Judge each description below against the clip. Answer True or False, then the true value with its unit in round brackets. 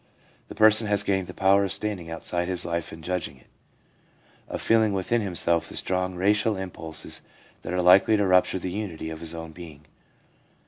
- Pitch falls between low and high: False (90 Hz)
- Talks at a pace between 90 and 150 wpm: False (185 wpm)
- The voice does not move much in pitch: False (3.2 semitones)